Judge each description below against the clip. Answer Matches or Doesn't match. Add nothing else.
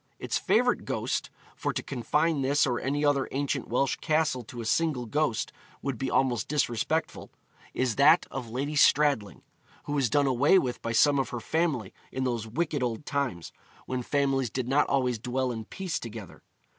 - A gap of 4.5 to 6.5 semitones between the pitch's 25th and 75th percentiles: Doesn't match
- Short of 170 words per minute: Doesn't match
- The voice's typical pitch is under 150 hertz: Matches